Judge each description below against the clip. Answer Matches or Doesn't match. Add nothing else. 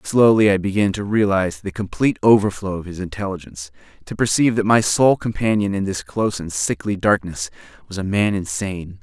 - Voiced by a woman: Doesn't match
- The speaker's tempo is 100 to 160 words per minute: Doesn't match